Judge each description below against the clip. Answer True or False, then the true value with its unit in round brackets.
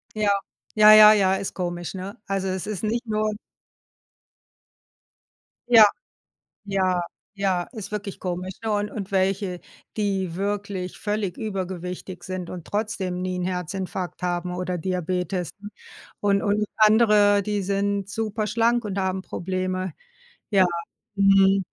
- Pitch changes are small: True (2.2 semitones)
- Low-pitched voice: False (195 Hz)